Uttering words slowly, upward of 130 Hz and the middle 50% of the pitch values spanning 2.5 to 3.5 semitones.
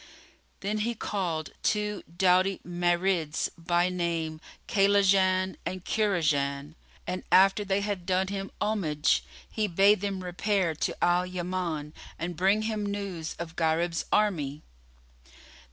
Yes: slow, 120 wpm; medium, 185 Hz; average, 2.9 semitones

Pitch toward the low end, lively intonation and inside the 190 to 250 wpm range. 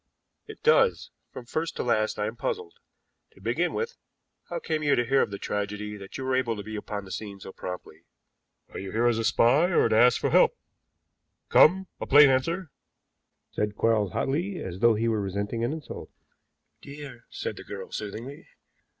Yes: low, 120 Hz; wide, 5.7 semitones; average, 195 wpm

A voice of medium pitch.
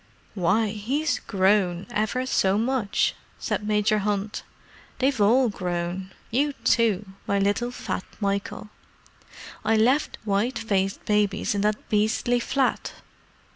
No: high, 210 Hz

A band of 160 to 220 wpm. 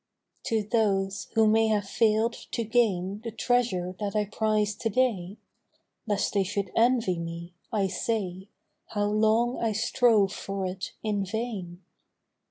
No: average, 145 wpm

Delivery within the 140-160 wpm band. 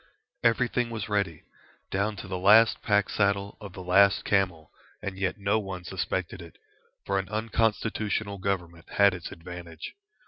Yes: average, 150 wpm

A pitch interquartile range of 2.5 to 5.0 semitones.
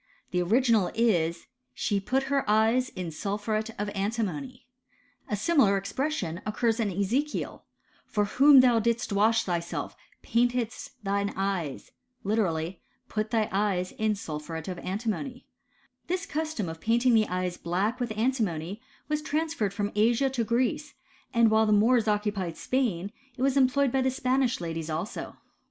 Yes: average, 4.5 semitones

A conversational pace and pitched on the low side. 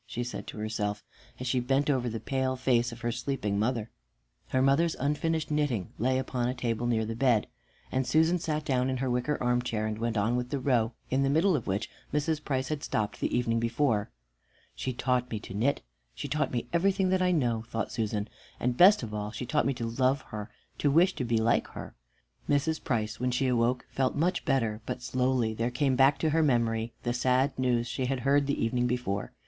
No: fast, 220 wpm; low, 125 Hz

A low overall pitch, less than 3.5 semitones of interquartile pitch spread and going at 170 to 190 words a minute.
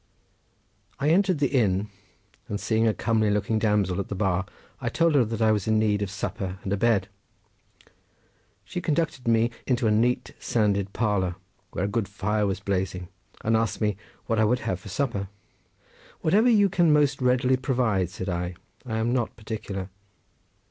No: low, 110 Hz; average, 4.0 semitones; average, 175 wpm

